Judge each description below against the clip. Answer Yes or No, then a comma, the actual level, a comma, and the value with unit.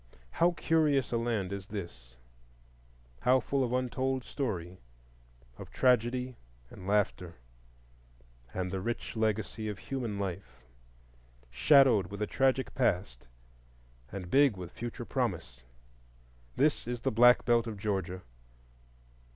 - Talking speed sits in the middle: No, slow, 120 wpm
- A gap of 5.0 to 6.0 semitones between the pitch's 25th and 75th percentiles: Yes, wide, 5.6 semitones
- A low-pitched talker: Yes, low, 105 Hz